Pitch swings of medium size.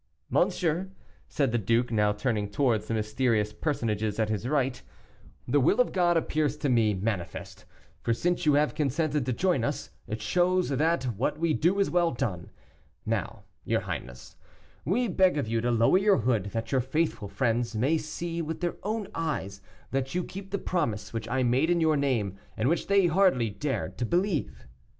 No: wide, 6.9 semitones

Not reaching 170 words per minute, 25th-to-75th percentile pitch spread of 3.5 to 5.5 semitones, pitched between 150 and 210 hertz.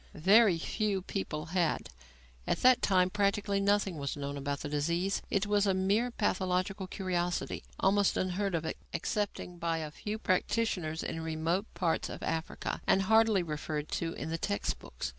Yes: average, 160 wpm; average, 3.8 semitones; medium, 185 Hz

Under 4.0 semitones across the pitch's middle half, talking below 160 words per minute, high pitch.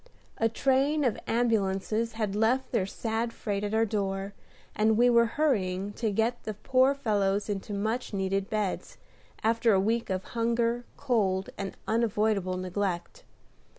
Yes: average, 2.9 semitones; average, 150 wpm; high, 220 Hz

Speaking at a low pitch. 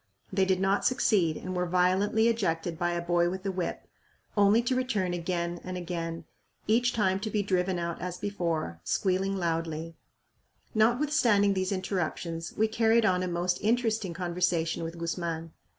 No: medium, 185 Hz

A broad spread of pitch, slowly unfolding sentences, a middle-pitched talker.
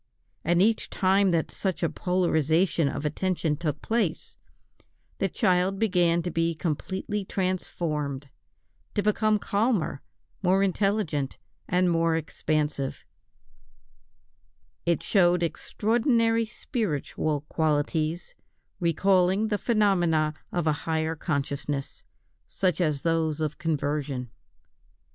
No: average, 4.0 semitones; slow, 105 wpm; medium, 170 Hz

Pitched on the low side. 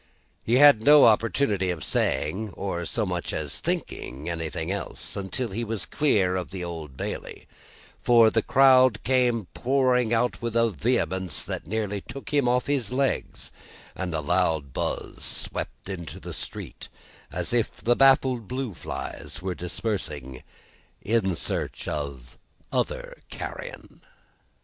Yes: low, 105 Hz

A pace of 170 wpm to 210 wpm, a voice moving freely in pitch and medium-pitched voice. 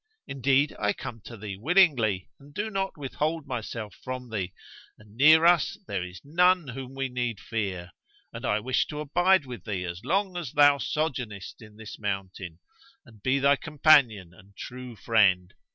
No: average, 175 wpm; wide, 6.3 semitones; low, 125 Hz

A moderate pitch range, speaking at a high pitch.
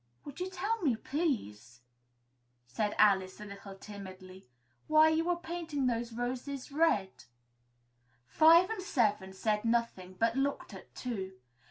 No: wide, 8.1 semitones; high, 235 Hz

